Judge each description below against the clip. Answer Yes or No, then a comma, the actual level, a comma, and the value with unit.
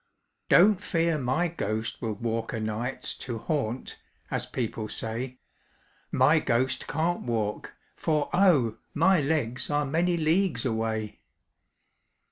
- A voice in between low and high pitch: No, low, 130 Hz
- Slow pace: Yes, slow, 120 wpm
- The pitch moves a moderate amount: No, wide, 6.1 semitones